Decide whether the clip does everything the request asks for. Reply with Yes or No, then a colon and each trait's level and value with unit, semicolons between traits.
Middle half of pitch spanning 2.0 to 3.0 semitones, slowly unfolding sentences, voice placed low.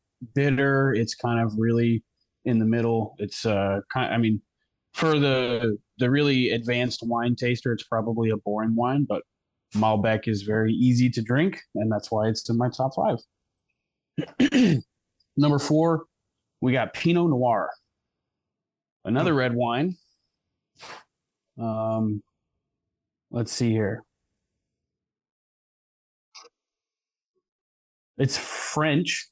No: average, 3.6 semitones; slow, 115 wpm; low, 120 Hz